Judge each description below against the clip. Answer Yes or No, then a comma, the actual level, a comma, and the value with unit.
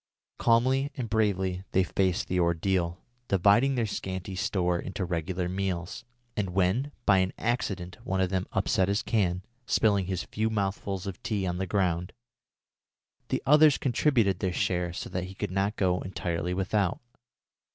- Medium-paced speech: Yes, average, 160 wpm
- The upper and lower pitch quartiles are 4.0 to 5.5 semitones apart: No, narrow, 2.6 semitones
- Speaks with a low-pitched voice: Yes, very low, 95 Hz